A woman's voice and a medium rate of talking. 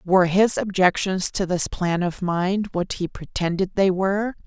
Yes: female; average, 175 wpm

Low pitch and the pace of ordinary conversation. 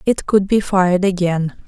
No: medium, 185 Hz; average, 180 wpm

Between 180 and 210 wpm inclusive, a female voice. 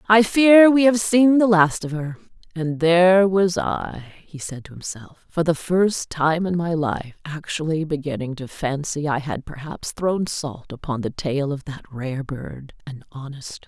Yes: average, 185 wpm; female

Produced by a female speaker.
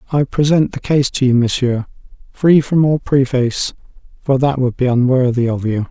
No: male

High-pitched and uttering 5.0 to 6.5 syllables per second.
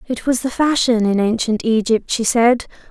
No: high, 230 Hz; 4.7 syllables/s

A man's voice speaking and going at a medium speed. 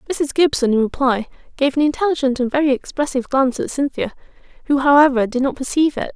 No: female; average, 185 wpm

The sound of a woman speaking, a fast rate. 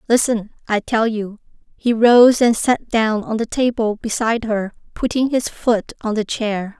No: female; average, 175 wpm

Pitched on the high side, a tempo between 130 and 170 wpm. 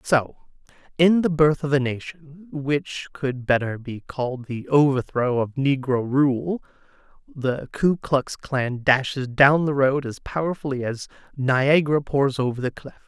No: medium, 140 Hz; average, 150 wpm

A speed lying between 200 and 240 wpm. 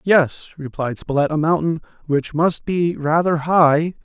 No: average, 150 wpm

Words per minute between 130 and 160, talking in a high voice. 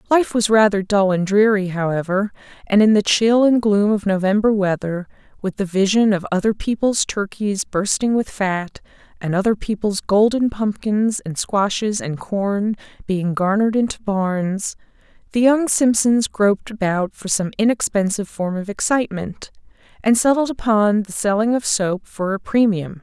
Yes: average, 155 wpm; high, 205 Hz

